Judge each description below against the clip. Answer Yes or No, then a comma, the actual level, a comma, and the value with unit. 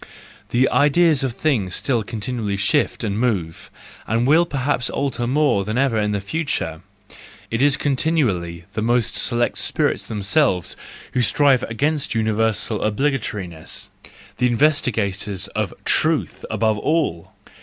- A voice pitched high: No, low, 115 Hz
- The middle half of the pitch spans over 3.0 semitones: Yes, average, 5.1 semitones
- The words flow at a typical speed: No, slow, 130 wpm